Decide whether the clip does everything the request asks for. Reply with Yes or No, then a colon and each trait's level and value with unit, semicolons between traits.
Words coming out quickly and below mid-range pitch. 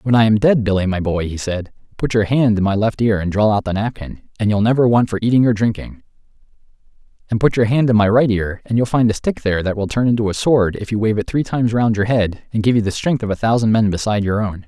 Yes: fast, 285 wpm; low, 110 Hz